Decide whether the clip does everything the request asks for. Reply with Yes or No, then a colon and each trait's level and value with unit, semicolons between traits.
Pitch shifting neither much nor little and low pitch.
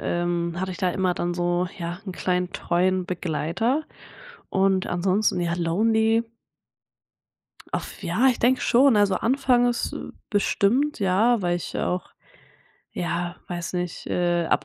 No: average, 4.1 semitones; medium, 185 Hz